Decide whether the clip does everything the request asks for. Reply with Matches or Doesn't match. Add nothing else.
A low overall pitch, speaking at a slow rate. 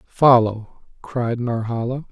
Matches